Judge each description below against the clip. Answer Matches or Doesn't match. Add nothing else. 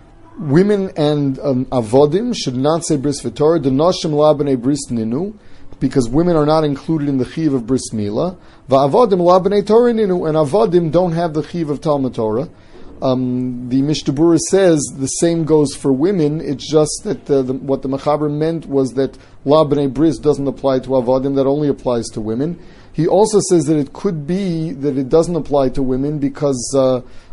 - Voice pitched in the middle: Matches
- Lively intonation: Doesn't match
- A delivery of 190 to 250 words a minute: Doesn't match